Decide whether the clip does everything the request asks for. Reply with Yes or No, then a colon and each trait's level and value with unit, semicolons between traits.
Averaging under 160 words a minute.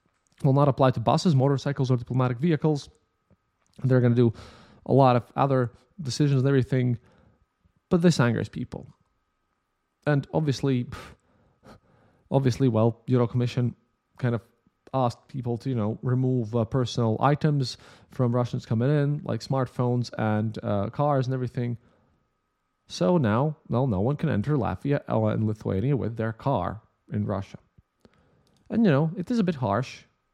Yes: average, 150 wpm